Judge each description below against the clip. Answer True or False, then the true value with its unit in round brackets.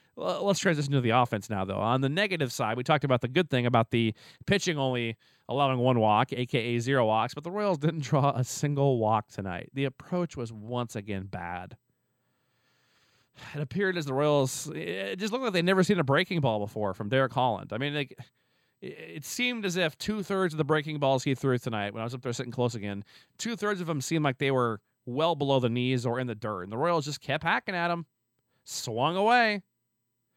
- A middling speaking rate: False (215 wpm)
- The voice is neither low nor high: False (130 Hz)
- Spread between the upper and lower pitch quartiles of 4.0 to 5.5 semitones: True (4.7 semitones)